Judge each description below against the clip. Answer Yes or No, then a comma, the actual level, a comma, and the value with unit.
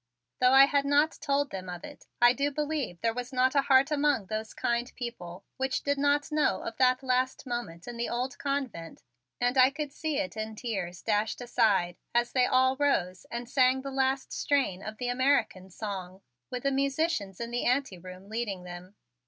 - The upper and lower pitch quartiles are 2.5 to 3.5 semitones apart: No, average, 4.7 semitones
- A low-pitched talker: No, very high, 250 Hz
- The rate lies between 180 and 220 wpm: Yes, average, 195 wpm